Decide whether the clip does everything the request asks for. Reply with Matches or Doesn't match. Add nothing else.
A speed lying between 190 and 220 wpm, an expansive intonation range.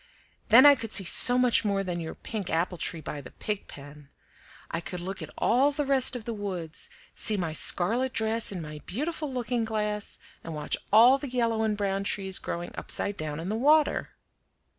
Matches